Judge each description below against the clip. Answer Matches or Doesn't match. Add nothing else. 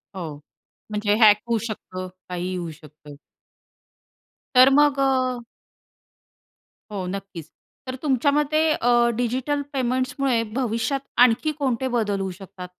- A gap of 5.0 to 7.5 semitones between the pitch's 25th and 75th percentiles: Matches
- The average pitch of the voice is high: Matches